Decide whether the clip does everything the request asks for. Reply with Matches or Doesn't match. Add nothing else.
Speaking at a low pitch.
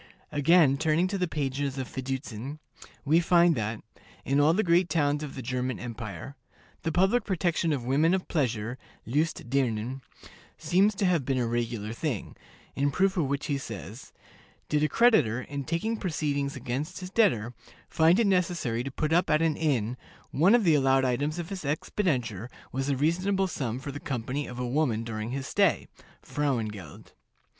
Doesn't match